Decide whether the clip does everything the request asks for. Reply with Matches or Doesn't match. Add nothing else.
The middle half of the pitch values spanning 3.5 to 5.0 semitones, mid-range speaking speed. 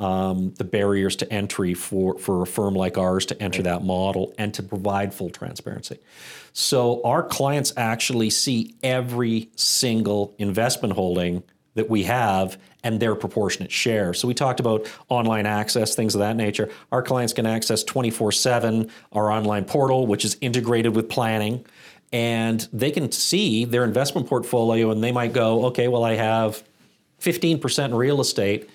Doesn't match